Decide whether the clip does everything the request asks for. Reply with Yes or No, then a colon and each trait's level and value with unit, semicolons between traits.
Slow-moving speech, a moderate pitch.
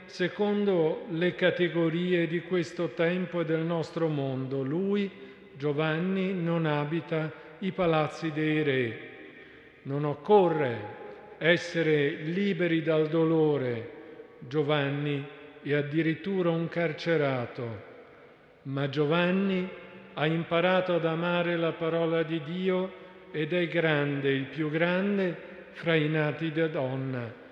Yes: slow, 110 wpm; medium, 165 Hz